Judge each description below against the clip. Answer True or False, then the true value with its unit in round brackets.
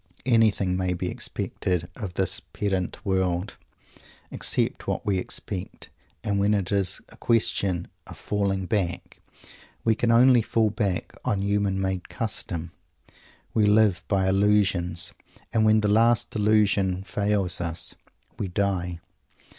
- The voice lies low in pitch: True (100 Hz)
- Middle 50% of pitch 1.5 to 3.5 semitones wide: True (2.4 semitones)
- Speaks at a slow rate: True (130 wpm)